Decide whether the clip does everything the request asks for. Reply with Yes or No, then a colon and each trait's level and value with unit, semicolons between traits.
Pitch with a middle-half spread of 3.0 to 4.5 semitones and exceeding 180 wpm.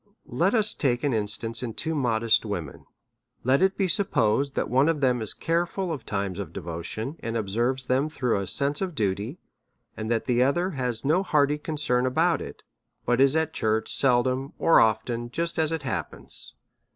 No: wide, 5.6 semitones; average, 190 wpm